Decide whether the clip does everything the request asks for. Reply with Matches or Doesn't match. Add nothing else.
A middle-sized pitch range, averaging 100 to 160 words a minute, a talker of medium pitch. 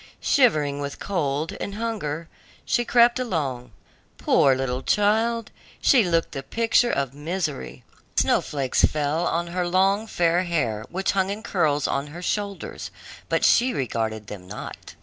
Doesn't match